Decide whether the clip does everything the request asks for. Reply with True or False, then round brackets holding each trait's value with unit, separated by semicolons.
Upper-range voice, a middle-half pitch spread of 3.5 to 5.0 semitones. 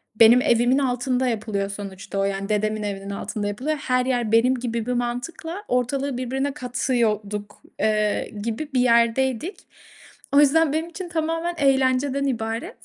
True (245 Hz; 4.2 semitones)